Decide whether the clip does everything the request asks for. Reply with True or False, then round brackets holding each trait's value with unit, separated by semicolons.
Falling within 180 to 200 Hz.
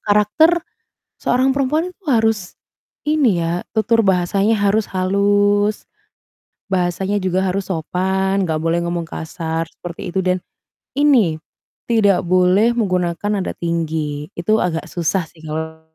True (190 Hz)